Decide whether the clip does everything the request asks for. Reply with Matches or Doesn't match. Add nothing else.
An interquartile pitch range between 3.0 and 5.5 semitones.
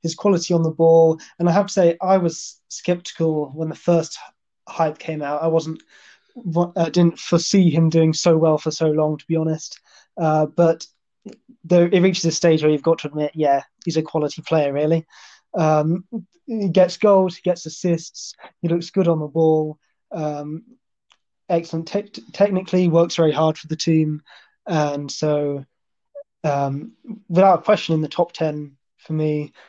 Doesn't match